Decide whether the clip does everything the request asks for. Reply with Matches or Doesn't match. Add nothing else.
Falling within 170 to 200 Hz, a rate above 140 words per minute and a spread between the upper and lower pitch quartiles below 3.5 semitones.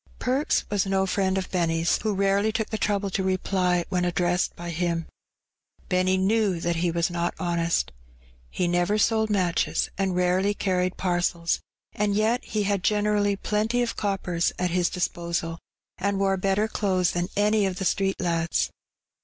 Matches